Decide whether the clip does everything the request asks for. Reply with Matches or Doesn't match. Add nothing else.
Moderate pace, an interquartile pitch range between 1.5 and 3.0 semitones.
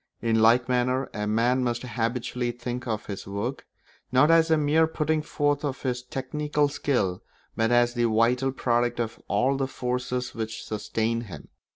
Matches